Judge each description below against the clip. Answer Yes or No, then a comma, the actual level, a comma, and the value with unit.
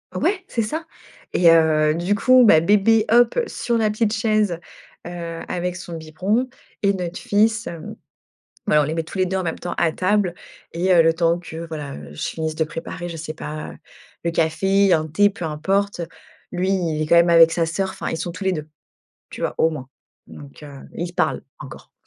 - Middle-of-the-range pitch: Yes, medium, 175 Hz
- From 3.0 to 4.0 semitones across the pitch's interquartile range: Yes, average, 3.7 semitones